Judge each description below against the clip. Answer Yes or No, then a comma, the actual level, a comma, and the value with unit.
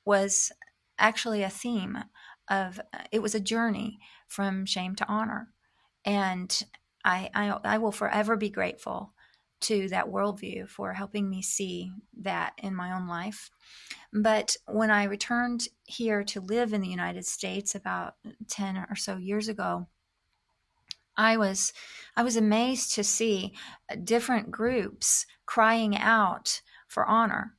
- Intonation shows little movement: Yes, narrow, 2.2 semitones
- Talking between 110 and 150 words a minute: Yes, slow, 135 wpm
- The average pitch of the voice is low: No, high, 210 Hz